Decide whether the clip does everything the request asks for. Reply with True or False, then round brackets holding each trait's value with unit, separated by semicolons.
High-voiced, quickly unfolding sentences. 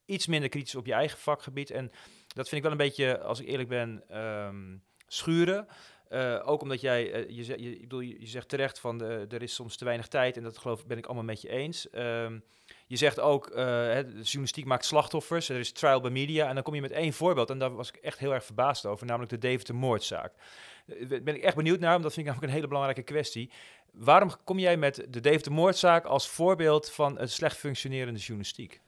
False (130 Hz; 240 wpm)